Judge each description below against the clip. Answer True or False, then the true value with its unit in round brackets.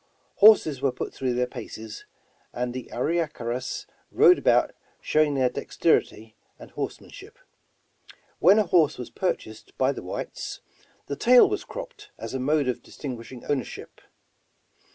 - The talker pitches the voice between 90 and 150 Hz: True (135 Hz)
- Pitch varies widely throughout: True (7.0 semitones)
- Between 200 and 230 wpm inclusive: False (150 wpm)